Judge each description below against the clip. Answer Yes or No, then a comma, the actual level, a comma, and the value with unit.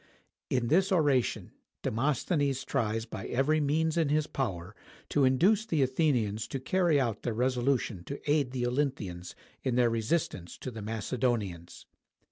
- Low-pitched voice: Yes, low, 130 Hz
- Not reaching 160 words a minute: Yes, average, 145 wpm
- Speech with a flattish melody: No, average, 4.5 semitones